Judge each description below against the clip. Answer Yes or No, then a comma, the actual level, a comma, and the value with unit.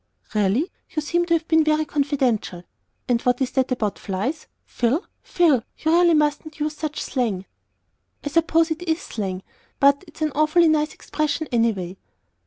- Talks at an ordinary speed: Yes, average, 165 wpm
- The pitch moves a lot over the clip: No, average, 5.0 semitones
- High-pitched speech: Yes, very high, 295 Hz